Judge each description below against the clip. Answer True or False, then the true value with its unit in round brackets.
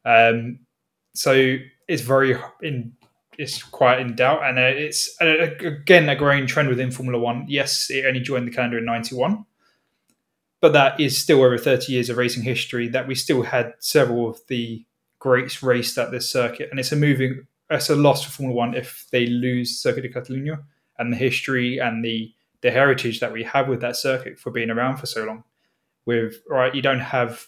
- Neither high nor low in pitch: False (125 Hz)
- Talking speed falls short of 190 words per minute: False (195 wpm)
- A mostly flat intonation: True (2.2 semitones)